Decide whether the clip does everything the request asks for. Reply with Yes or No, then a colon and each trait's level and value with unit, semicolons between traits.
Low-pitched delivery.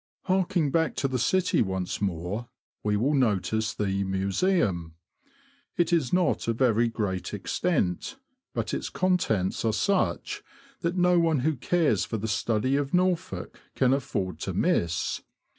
Yes: low, 120 Hz